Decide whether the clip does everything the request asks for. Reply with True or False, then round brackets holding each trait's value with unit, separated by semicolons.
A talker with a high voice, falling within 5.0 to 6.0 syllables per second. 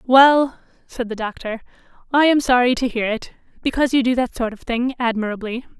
True (245 Hz; 5.6 syllables/s)